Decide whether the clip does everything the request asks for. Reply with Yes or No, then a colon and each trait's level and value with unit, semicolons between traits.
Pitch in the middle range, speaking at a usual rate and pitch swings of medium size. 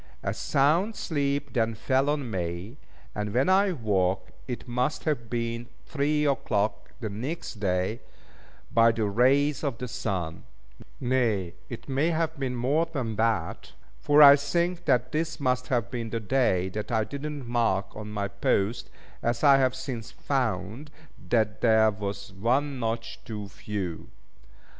No: low, 120 Hz; average, 155 wpm; average, 4.8 semitones